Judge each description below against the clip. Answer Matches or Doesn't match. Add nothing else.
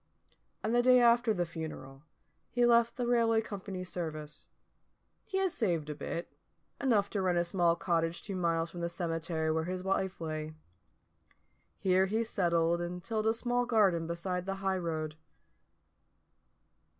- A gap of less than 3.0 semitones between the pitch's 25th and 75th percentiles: Doesn't match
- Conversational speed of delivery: Matches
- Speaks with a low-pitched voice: Doesn't match